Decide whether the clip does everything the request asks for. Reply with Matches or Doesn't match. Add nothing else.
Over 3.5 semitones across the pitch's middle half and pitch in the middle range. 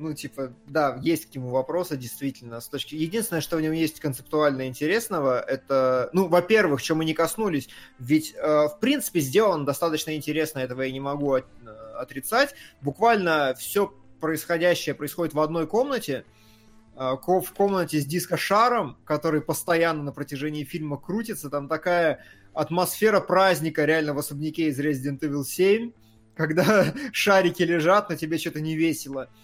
Matches